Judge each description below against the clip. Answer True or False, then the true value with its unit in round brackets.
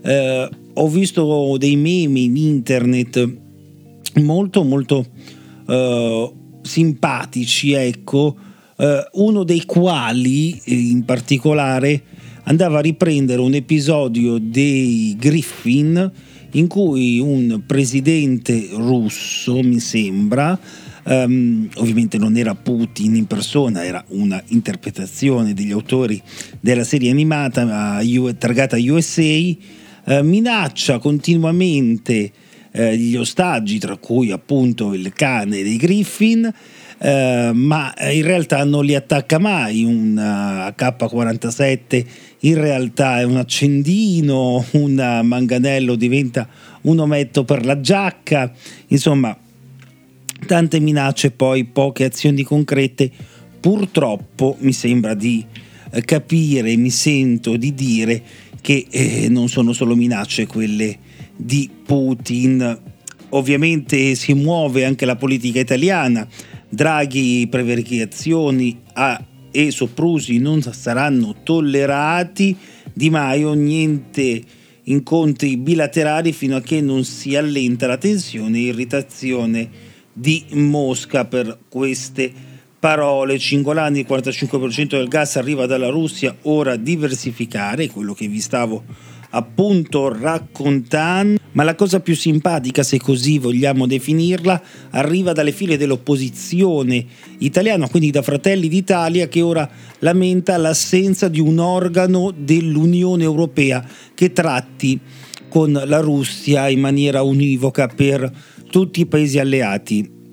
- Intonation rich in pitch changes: False (4.1 semitones)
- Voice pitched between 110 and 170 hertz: True (140 Hz)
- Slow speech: True (110 wpm)